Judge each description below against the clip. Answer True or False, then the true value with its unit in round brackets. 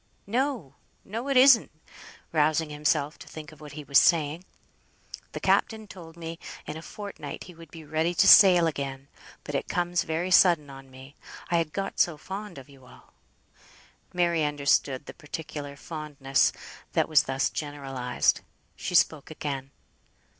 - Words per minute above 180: False (155 wpm)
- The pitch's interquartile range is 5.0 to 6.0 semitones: False (3.7 semitones)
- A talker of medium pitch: True (155 Hz)